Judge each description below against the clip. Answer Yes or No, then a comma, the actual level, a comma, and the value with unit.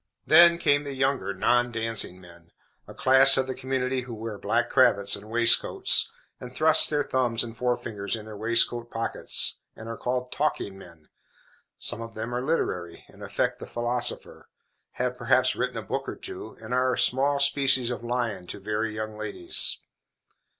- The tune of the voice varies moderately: Yes, average, 3.4 semitones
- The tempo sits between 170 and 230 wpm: Yes, average, 175 wpm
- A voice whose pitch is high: No, low, 120 Hz